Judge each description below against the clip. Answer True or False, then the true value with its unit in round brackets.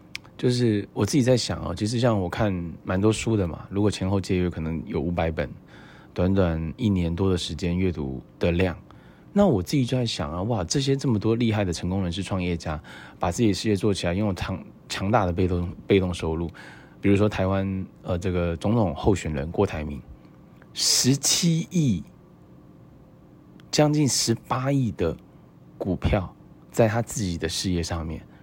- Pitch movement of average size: True (4.6 semitones)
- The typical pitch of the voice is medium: False (95 Hz)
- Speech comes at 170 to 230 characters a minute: False (260 characters per minute)